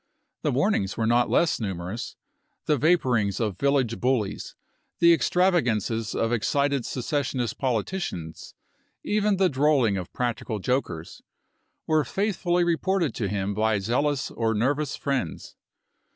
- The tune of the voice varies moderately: No, wide, 6.0 semitones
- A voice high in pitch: No, low, 125 Hz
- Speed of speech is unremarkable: No, slow, 125 wpm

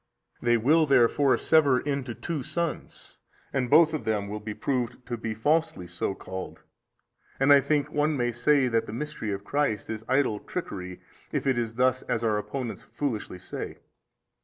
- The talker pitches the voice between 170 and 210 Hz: No, low, 125 Hz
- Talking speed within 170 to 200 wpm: Yes, average, 180 wpm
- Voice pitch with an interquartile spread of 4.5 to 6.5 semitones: Yes, average, 4.8 semitones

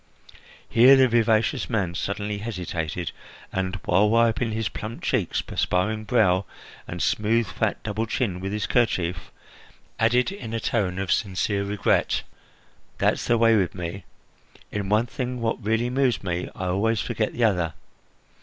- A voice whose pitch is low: Yes, low, 110 Hz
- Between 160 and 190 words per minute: No, average, 150 wpm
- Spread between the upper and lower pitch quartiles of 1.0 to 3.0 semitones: No, average, 3.6 semitones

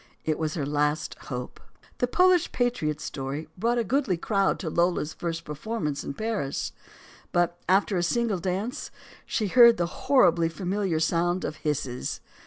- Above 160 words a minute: No, average, 155 wpm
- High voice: No, medium, 175 Hz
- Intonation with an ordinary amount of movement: No, wide, 6.1 semitones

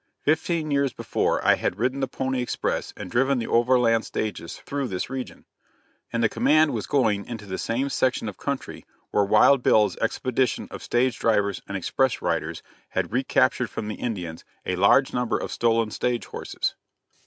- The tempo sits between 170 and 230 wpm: Yes, average, 175 wpm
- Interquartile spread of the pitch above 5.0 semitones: No, average, 3.8 semitones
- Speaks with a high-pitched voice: No, low, 120 Hz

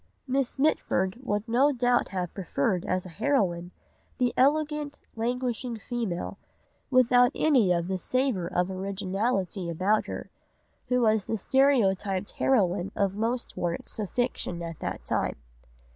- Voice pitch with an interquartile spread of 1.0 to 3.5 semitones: No, average, 5.3 semitones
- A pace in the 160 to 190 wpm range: No, slow, 135 wpm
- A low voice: No, high, 215 Hz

